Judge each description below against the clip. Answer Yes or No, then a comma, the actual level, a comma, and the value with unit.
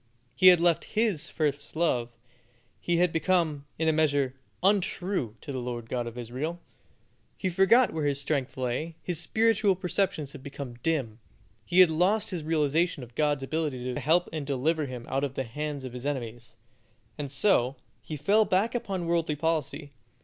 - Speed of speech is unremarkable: Yes, average, 175 wpm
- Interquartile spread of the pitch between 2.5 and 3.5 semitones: No, average, 4.7 semitones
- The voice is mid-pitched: Yes, medium, 155 Hz